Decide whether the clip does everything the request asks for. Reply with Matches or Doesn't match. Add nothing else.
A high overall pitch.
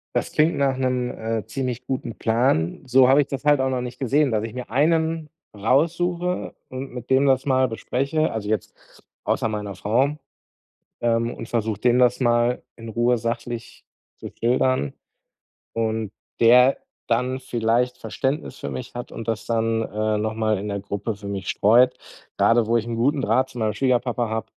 Doesn't match